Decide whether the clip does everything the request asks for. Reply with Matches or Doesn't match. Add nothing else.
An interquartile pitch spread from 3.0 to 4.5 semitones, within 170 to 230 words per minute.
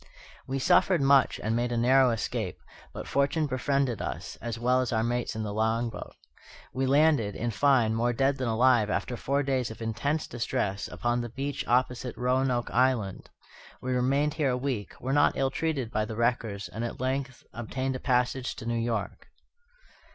Doesn't match